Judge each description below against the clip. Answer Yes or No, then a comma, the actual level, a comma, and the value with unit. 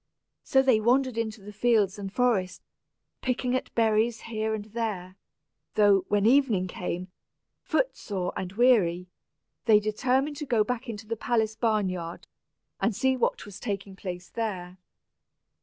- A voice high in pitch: Yes, high, 215 Hz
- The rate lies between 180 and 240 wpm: No, average, 145 wpm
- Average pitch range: Yes, average, 3.7 semitones